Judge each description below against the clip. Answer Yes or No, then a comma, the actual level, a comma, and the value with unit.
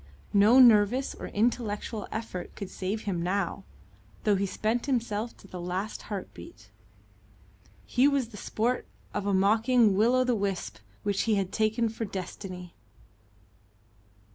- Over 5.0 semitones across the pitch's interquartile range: No, average, 3.1 semitones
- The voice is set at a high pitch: Yes, high, 210 Hz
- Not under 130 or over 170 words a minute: Yes, average, 140 wpm